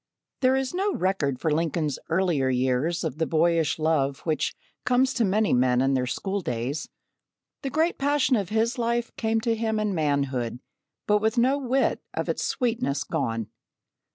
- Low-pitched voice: No, medium, 180 Hz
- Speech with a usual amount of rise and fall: No, wide, 9.0 semitones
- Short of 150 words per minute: No, average, 170 wpm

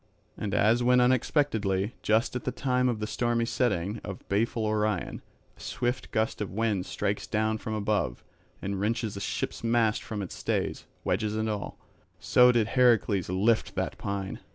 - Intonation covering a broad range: No, average, 2.7 semitones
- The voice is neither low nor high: No, low, 110 Hz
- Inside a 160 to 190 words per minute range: Yes, average, 170 wpm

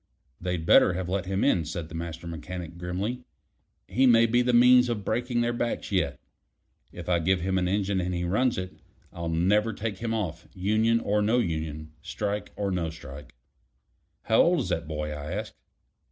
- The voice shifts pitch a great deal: No, average, 4.9 semitones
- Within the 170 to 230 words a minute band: Yes, average, 190 wpm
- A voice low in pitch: Yes, very low, 95 Hz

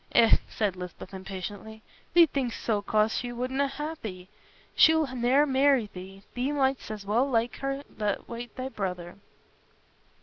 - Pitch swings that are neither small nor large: Yes, average, 5.0 semitones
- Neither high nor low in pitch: No, high, 235 Hz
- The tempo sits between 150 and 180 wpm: Yes, average, 155 wpm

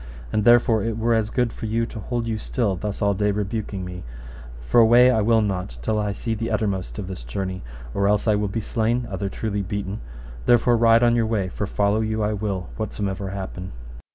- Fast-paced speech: Yes, fast, 215 wpm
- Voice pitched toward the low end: Yes, low, 105 Hz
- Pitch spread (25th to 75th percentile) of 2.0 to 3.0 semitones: Yes, narrow, 2.6 semitones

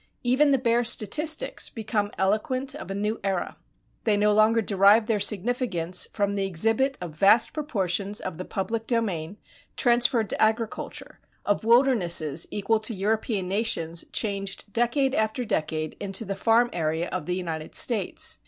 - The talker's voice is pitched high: Yes, high, 210 Hz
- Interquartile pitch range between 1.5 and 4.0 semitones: Yes, average, 3.5 semitones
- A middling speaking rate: Yes, average, 155 wpm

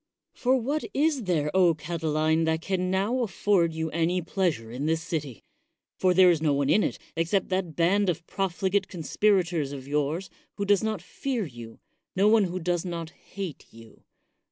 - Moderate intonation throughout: Yes, average, 3.6 semitones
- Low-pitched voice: No, medium, 175 Hz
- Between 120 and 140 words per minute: No, average, 180 wpm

